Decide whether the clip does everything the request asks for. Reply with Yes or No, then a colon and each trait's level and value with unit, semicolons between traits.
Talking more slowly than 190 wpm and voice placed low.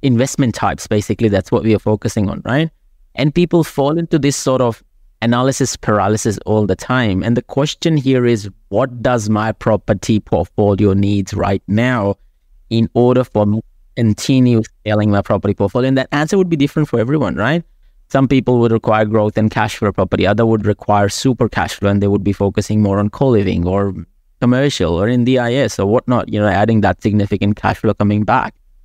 No: average, 195 wpm; low, 110 Hz